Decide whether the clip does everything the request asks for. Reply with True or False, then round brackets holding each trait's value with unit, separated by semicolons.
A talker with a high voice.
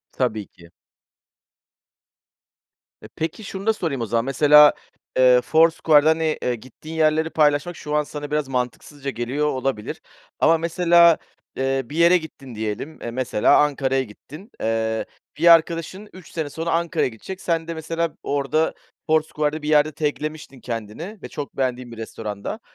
False (150 Hz)